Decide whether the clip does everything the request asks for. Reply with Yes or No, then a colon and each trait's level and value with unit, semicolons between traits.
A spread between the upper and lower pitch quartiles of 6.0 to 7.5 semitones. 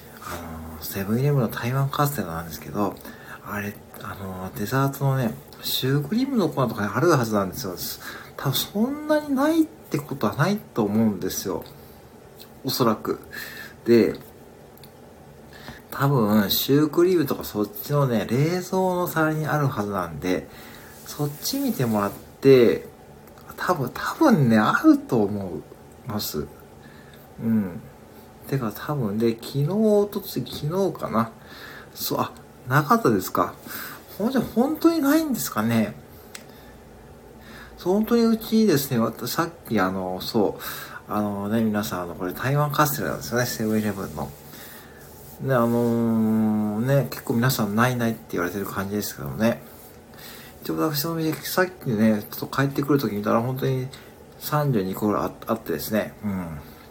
Yes: wide, 6.7 semitones